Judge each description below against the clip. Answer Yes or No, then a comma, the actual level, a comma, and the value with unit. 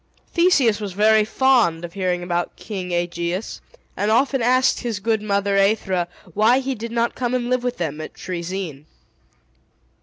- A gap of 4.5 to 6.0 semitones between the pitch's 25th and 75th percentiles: Yes, average, 5.2 semitones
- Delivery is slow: No, average, 160 wpm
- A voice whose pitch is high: Yes, high, 210 Hz